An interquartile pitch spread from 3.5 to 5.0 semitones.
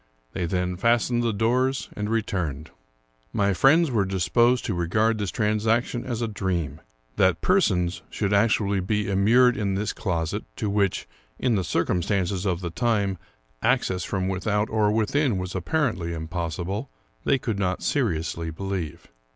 Yes: average, 3.9 semitones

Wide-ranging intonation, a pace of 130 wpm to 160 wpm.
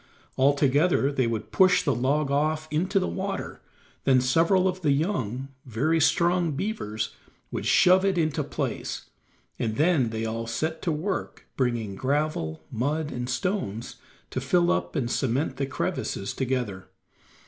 Yes: wide, 5.9 semitones; average, 145 wpm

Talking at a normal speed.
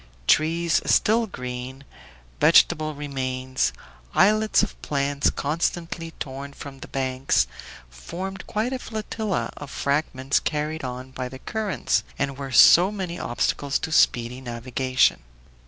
No: slow, 120 wpm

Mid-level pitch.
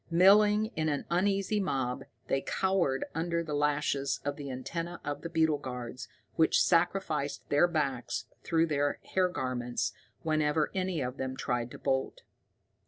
Yes: medium, 150 Hz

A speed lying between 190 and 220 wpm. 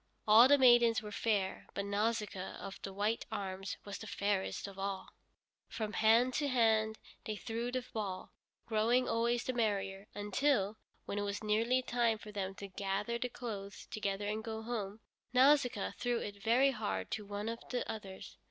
No: average, 175 wpm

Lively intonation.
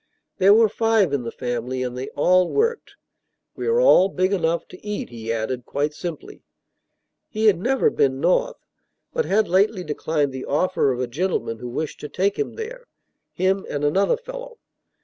Yes: wide, 8.2 semitones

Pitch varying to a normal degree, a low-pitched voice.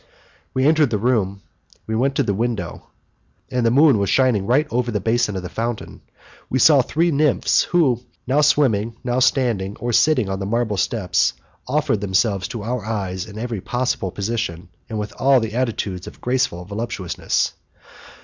Yes: average, 4.2 semitones; low, 115 Hz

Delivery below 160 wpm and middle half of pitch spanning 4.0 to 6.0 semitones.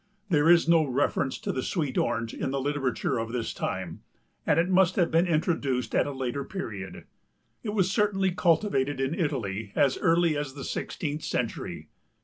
No: average, 175 wpm; average, 4.7 semitones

